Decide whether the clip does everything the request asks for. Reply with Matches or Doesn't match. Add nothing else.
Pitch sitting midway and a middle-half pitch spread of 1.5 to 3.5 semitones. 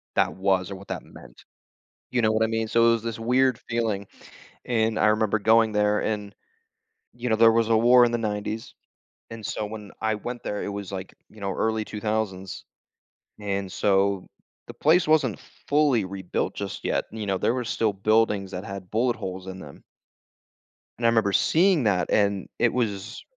Doesn't match